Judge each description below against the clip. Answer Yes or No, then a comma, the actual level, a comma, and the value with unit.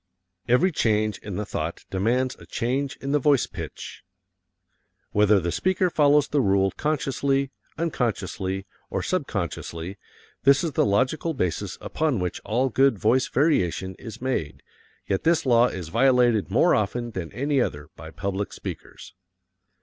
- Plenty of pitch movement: Yes, wide, 6.0 semitones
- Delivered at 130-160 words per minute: Yes, average, 145 wpm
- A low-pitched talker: Yes, low, 120 Hz